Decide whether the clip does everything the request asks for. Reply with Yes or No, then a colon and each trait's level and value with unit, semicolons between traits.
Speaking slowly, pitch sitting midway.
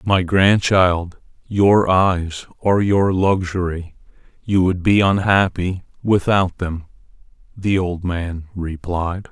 No: slow, 110 wpm; very low, 90 Hz